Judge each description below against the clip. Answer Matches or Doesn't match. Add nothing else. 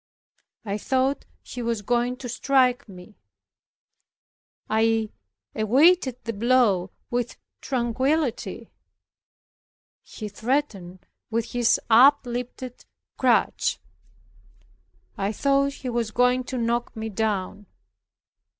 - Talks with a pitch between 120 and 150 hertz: Doesn't match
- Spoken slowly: Matches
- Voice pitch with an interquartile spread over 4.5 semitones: Doesn't match